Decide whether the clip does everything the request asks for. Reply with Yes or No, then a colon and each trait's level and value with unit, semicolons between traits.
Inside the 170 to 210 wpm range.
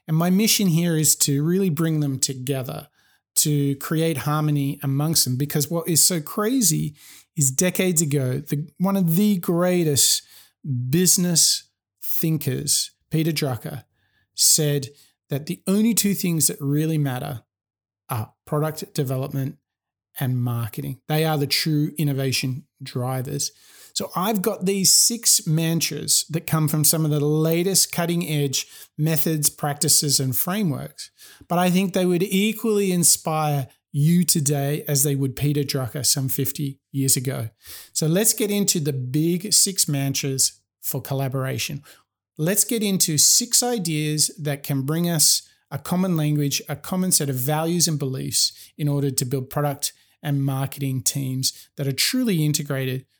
No: average, 145 wpm